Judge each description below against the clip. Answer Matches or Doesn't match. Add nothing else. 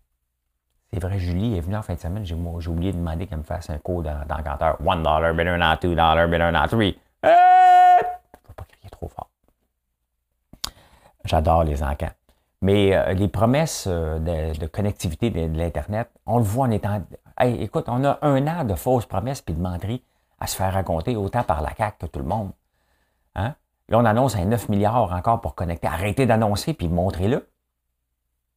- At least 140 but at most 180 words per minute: Doesn't match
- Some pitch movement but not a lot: Doesn't match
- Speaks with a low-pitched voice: Matches